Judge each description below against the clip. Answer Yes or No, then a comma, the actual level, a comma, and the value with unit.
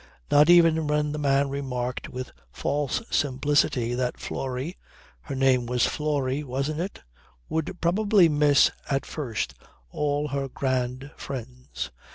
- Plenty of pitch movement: No, average, 2.7 semitones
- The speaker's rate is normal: No, slow, 130 wpm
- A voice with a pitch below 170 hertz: Yes, medium, 140 Hz